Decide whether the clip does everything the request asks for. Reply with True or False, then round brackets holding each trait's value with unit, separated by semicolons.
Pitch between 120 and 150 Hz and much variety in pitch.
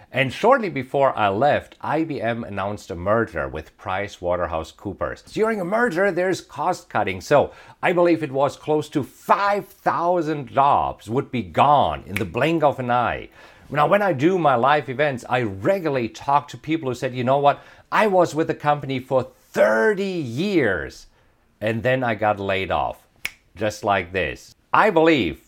True (135 Hz; 5.9 semitones)